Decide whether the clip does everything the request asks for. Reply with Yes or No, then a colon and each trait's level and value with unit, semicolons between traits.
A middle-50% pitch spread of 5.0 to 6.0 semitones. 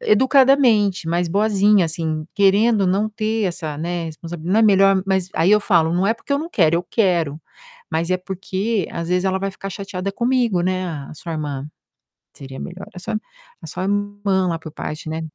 No: average, 3.5 semitones